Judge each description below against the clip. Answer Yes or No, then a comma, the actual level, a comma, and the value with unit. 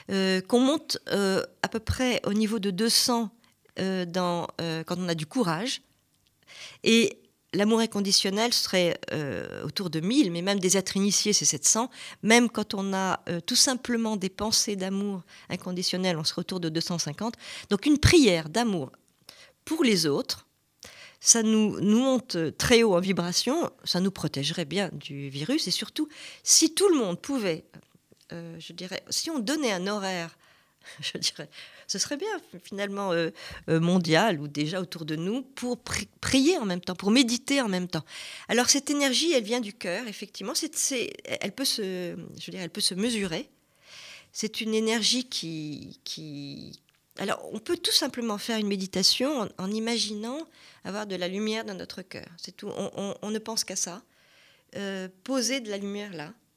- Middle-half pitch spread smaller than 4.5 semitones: No, average, 4.9 semitones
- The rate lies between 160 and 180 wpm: Yes, average, 175 wpm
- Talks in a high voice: Yes, high, 200 Hz